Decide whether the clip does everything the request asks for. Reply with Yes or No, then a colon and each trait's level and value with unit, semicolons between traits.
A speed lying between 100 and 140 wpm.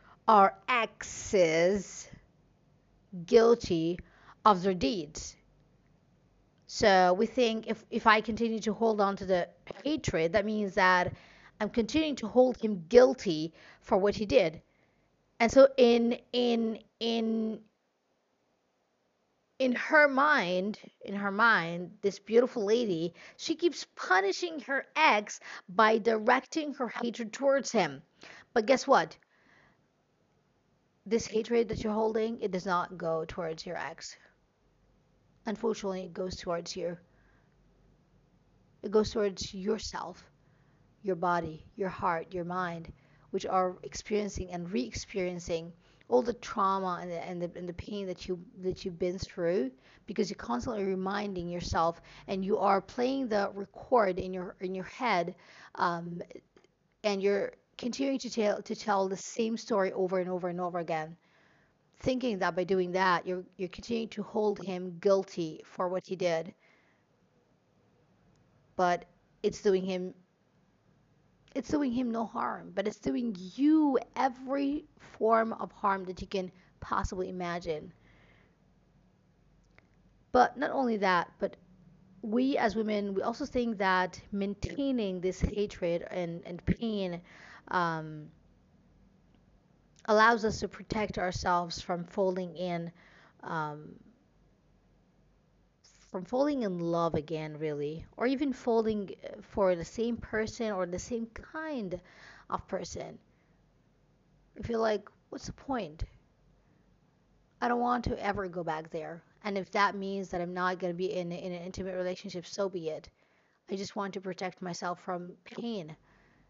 Yes: slow, 135 wpm